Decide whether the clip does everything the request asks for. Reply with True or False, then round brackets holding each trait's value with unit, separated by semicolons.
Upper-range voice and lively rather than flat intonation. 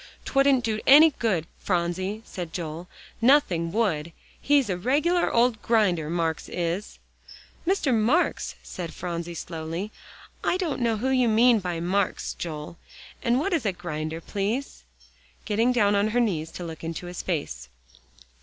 True (200 Hz; 6.2 semitones)